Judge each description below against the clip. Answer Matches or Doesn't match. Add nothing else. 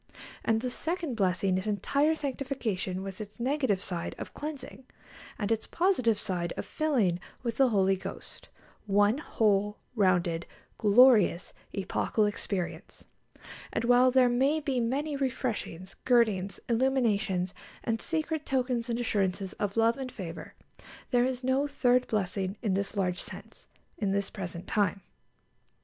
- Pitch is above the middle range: Matches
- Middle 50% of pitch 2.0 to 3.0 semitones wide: Doesn't match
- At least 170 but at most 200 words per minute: Doesn't match